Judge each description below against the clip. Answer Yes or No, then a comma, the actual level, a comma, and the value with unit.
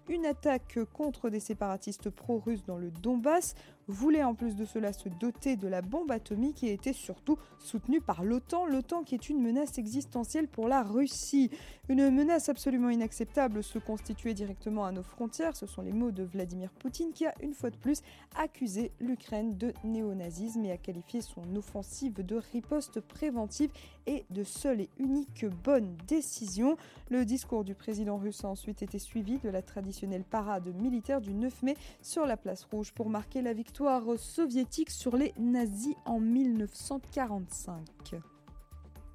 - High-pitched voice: Yes, high, 235 Hz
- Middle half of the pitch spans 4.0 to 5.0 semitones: Yes, average, 4.7 semitones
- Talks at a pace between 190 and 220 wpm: No, average, 165 wpm